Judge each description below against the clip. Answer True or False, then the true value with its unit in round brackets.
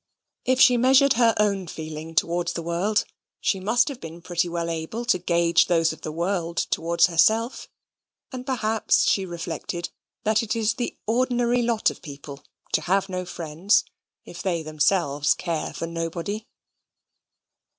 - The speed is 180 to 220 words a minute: False (155 wpm)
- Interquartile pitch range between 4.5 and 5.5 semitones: True (5.0 semitones)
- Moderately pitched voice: True (180 Hz)